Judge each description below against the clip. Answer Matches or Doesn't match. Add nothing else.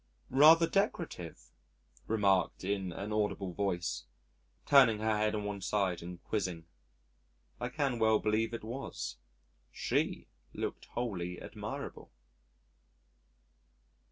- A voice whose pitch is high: Doesn't match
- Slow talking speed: Matches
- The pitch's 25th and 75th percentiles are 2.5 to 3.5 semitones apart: Doesn't match